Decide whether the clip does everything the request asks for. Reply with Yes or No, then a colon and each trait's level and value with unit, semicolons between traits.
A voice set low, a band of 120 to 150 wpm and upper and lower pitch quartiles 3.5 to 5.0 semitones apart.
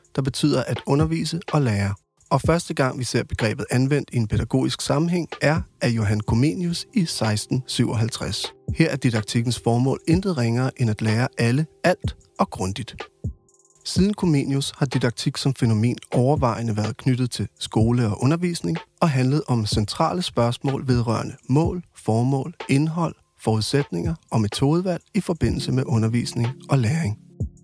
Yes: low, 130 Hz; slow, 145 wpm; average, 4.6 semitones